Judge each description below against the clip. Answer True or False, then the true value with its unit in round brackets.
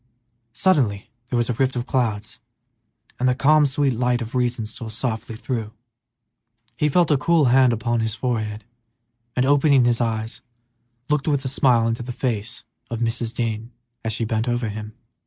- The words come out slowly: False (175 wpm)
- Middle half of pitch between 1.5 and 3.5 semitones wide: True (2.7 semitones)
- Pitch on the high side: False (120 Hz)